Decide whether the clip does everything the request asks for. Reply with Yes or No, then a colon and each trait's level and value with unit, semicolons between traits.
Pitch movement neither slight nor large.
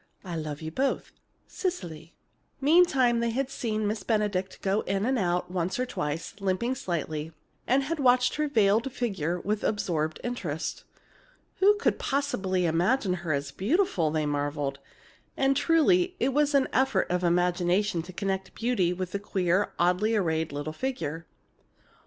No: wide, 6.9 semitones